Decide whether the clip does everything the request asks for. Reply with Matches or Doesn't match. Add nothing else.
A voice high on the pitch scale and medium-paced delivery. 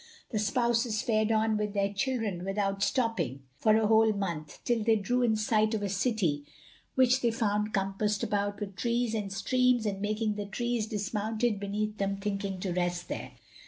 Matches